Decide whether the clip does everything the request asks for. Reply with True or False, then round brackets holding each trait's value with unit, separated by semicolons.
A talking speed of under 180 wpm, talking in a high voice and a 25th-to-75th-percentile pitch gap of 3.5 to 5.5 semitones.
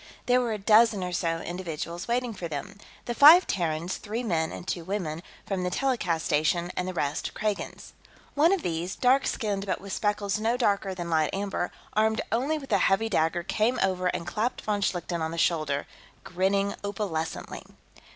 False (185 wpm; 195 Hz; 4.3 semitones)